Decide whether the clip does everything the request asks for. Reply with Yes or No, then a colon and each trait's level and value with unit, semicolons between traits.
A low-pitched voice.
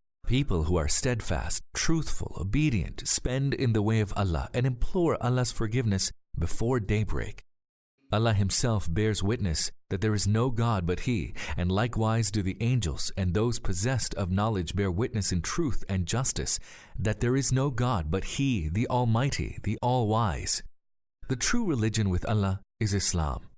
Yes: low, 110 Hz